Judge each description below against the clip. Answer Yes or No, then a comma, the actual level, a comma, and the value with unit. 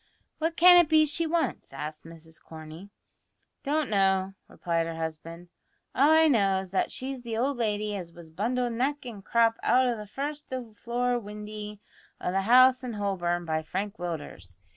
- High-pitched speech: Yes, high, 210 Hz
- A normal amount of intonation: No, wide, 6.7 semitones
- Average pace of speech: Yes, average, 175 wpm